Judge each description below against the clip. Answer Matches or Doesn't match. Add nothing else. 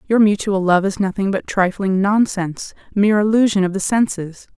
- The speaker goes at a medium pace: Matches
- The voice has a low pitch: Doesn't match